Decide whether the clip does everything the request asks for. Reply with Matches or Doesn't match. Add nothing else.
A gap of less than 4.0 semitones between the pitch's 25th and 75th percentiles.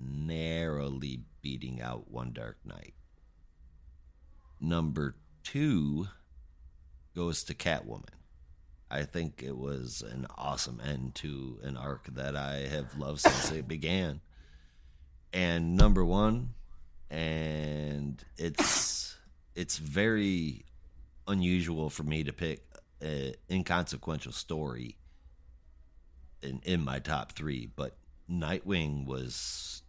Matches